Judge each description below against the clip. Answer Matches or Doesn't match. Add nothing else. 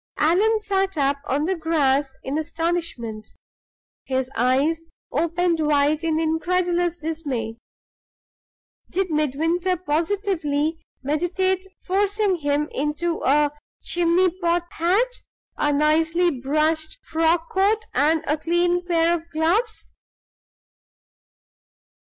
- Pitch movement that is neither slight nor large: Matches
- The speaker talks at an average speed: Doesn't match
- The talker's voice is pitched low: Doesn't match